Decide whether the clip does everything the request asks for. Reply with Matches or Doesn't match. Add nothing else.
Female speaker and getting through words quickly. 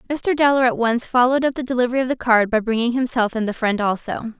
Matches